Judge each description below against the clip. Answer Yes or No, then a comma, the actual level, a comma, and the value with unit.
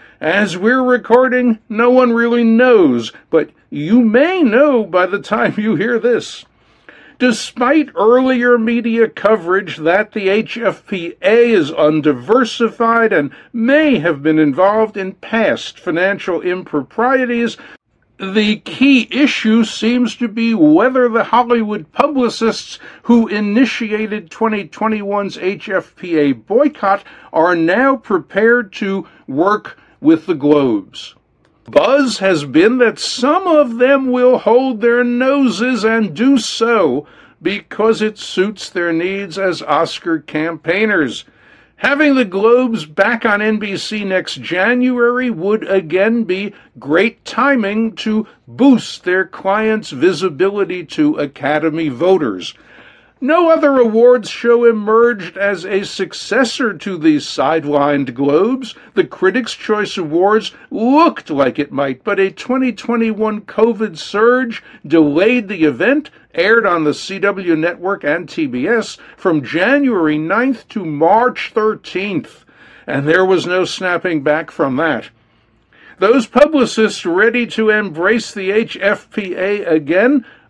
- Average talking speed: No, slow, 120 wpm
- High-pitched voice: Yes, high, 220 Hz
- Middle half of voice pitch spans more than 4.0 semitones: Yes, average, 4.7 semitones